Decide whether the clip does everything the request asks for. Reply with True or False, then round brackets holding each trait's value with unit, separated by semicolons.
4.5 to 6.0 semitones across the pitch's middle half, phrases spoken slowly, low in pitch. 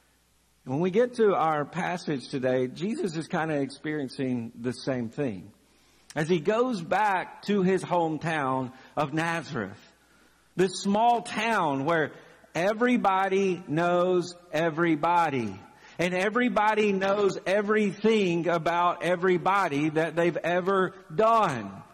False (4.9 semitones; 110 wpm; 175 Hz)